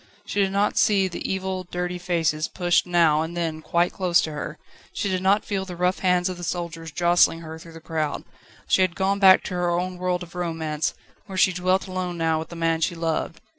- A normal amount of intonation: No, narrow, 2.1 semitones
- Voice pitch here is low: No, medium, 175 Hz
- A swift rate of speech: Yes, fast, 225 wpm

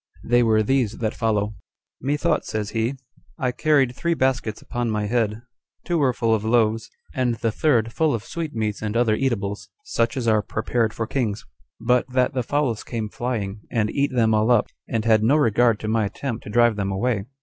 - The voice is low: Yes, low, 115 Hz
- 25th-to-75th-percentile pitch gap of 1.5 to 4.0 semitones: Yes, average, 2.8 semitones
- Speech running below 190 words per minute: No, average, 195 wpm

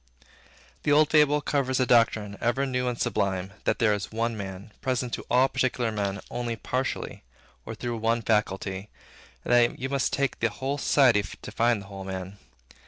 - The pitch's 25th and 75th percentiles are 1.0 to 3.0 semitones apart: No, average, 3.9 semitones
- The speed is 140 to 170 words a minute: No, average, 180 wpm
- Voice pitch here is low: Yes, low, 115 Hz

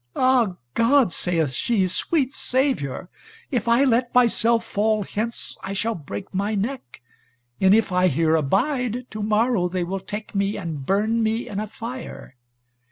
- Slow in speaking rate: No, average, 160 wpm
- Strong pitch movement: No, average, 4.4 semitones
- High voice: Yes, high, 215 Hz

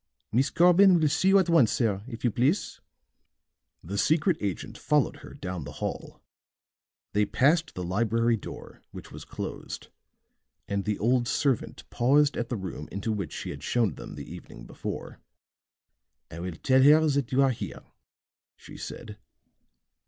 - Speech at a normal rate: Yes, average, 160 wpm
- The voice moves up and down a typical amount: No, wide, 6.4 semitones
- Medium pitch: No, low, 120 Hz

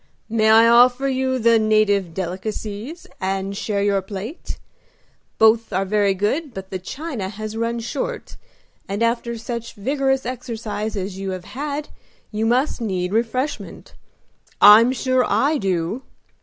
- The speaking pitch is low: No, high, 220 Hz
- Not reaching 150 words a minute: Yes, average, 140 wpm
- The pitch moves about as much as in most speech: Yes, average, 4.1 semitones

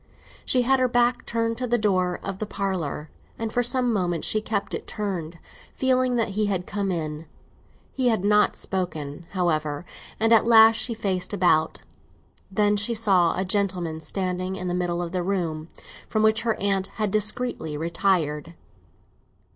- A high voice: Yes, high, 195 Hz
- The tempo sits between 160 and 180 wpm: Yes, average, 170 wpm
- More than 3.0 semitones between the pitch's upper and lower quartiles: Yes, average, 4.1 semitones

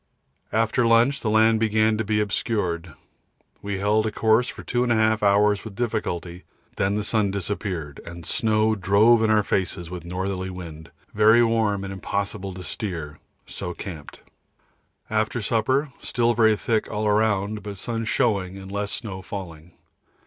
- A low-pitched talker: Yes, low, 105 Hz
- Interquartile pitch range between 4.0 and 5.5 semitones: No, average, 2.7 semitones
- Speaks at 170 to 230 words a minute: No, average, 155 wpm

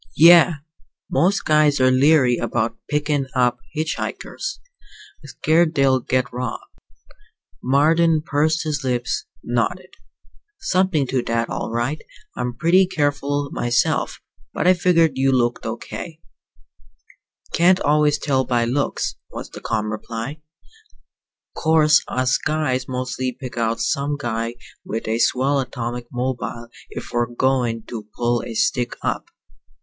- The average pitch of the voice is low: Yes, low, 130 Hz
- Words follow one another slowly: Yes, slow, 130 wpm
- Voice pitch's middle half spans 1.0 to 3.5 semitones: No, average, 4.2 semitones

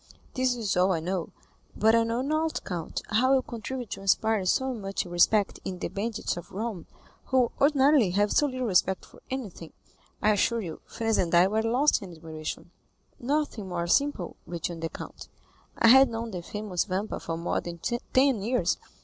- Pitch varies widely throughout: Yes, wide, 5.7 semitones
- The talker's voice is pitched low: No, high, 215 Hz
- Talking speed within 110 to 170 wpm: No, average, 185 wpm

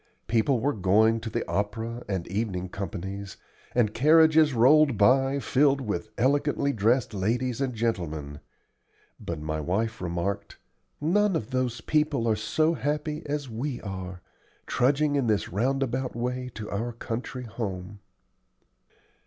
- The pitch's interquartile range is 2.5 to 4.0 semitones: No, average, 5.2 semitones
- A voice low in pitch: Yes, low, 115 Hz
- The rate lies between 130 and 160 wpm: Yes, slow, 135 wpm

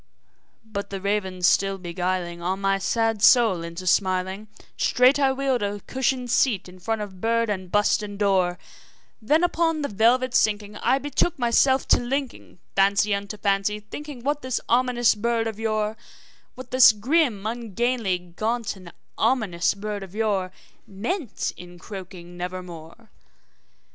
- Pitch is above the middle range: Yes, high, 210 Hz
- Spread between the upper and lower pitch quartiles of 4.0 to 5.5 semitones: Yes, average, 4.3 semitones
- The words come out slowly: No, average, 155 wpm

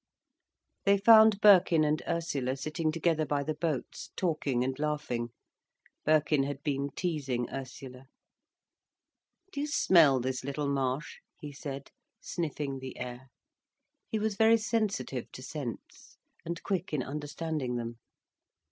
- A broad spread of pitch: No, average, 4.1 semitones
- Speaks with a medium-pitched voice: Yes, medium, 150 Hz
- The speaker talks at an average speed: No, slow, 130 wpm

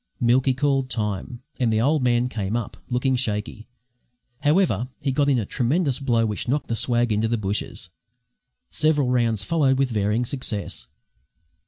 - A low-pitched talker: Yes, low, 120 Hz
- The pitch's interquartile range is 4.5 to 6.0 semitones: No, average, 3.4 semitones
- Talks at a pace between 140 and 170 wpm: Yes, average, 160 wpm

